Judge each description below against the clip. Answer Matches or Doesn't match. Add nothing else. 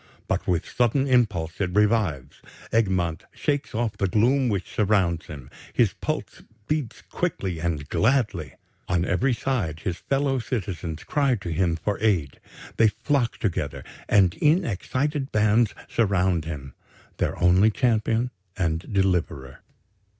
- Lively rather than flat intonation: Matches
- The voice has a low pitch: Matches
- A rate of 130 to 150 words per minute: Matches